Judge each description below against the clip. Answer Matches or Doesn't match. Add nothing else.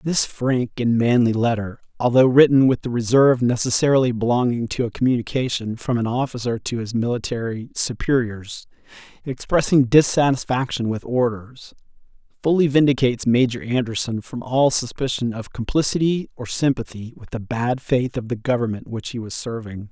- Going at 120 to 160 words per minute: Matches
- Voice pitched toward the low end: Matches